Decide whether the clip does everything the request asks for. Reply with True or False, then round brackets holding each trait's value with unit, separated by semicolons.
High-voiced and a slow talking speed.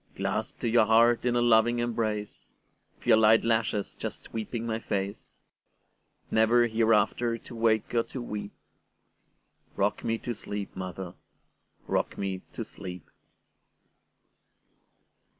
False (110 Hz; 110 wpm)